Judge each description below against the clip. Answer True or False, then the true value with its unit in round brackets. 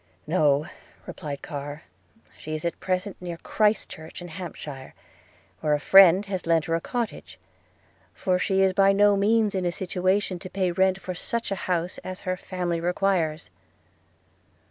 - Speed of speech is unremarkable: True (160 wpm)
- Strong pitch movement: False (2.8 semitones)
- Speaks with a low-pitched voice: False (180 Hz)